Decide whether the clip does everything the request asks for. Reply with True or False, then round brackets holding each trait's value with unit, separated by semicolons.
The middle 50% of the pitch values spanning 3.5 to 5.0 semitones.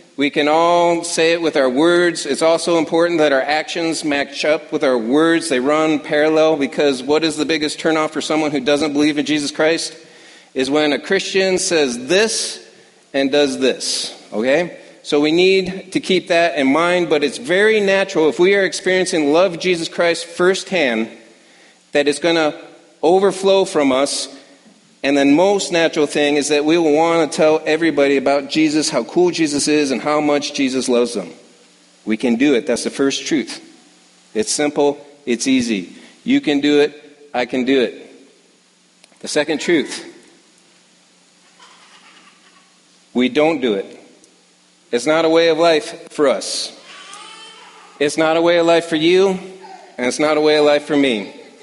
False (2.8 semitones)